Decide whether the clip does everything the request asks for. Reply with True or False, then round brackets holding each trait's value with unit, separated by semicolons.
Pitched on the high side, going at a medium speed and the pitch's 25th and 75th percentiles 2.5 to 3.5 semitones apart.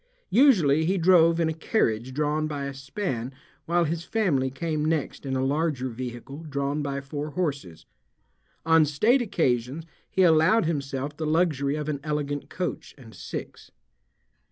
False (150 Hz; 155 wpm; 3.2 semitones)